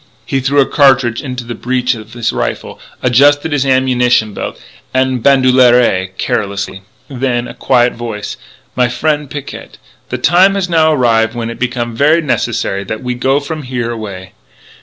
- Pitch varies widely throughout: No, average, 2.7 semitones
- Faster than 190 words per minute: No, average, 165 wpm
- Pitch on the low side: Yes, low, 125 Hz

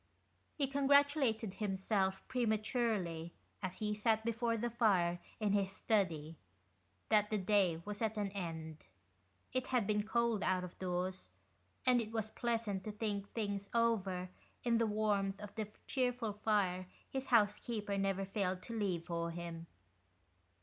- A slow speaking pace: No, average, 145 wpm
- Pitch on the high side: Yes, high, 210 Hz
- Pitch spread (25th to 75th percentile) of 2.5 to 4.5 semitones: Yes, average, 3.4 semitones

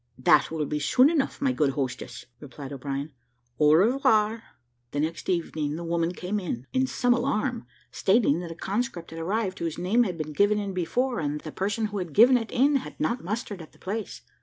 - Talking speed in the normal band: No, fast, 210 wpm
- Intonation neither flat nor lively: No, wide, 6.7 semitones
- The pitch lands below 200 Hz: Yes, medium, 185 Hz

